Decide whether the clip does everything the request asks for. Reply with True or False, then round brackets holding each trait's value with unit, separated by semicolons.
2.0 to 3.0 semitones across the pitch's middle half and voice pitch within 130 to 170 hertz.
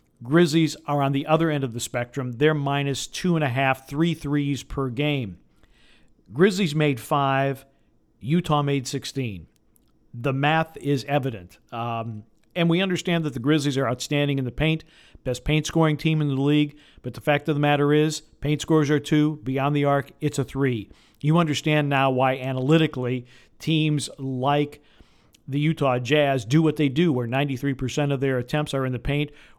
True (2.5 semitones; 140 Hz)